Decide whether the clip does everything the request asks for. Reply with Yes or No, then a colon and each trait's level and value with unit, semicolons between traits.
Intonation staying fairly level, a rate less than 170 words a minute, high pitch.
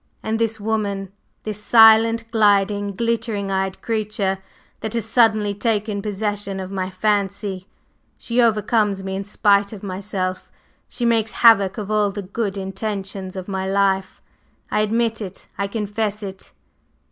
Yes: narrow, 2.2 semitones; average, 145 wpm; high, 205 Hz